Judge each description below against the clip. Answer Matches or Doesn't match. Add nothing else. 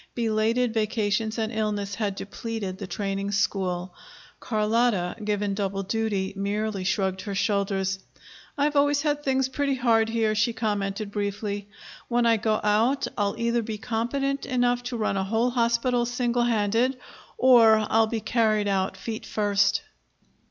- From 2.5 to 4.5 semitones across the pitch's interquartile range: Matches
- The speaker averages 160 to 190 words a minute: Doesn't match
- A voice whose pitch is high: Matches